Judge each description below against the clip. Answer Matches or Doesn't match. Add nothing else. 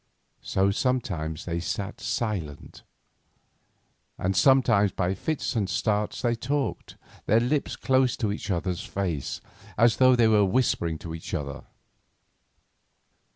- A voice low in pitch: Matches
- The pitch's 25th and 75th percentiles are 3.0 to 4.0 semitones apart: Doesn't match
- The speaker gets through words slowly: Matches